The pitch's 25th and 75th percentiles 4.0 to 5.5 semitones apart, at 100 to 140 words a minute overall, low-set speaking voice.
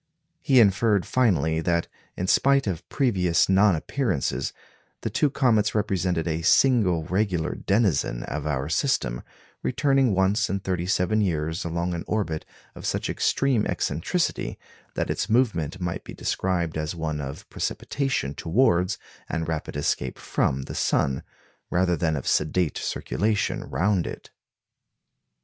Yes: average, 5.0 semitones; slow, 135 wpm; very low, 90 Hz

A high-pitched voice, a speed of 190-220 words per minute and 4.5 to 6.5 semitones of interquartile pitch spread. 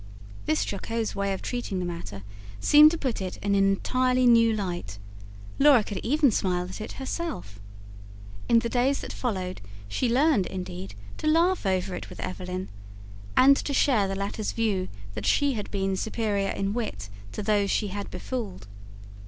No: high, 205 Hz; average, 170 wpm; average, 5.1 semitones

